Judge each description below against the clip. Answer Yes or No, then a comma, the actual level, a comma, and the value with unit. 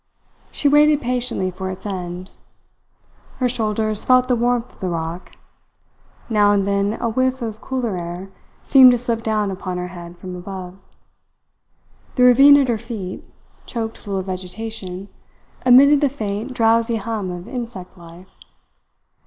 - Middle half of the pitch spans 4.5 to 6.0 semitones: Yes, average, 4.8 semitones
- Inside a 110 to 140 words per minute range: No, average, 150 wpm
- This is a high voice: Yes, high, 215 Hz